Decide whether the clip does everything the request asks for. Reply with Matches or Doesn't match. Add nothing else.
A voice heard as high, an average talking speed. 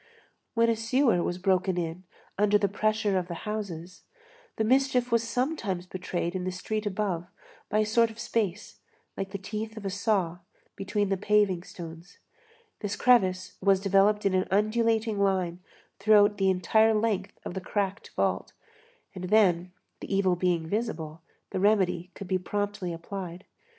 Matches